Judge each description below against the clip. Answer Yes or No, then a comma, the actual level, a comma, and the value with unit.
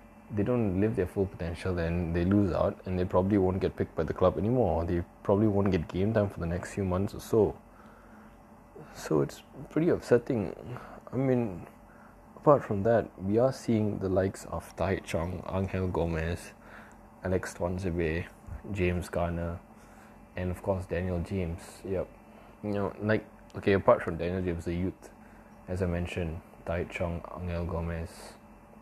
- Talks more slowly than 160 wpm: No, average, 165 wpm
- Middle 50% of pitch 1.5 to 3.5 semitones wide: Yes, average, 3.2 semitones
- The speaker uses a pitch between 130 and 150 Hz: No, very low, 95 Hz